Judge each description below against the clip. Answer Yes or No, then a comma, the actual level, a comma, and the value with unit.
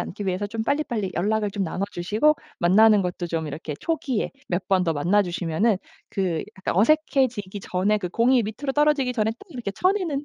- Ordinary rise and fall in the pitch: No, wide, 5.8 semitones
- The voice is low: No, high, 210 Hz